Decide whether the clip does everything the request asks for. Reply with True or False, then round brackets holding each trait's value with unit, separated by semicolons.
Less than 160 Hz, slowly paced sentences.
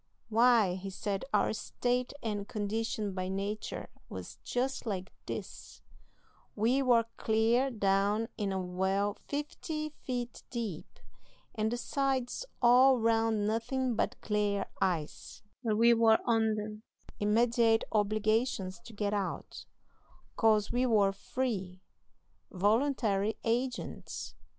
False (220 Hz; 115 wpm)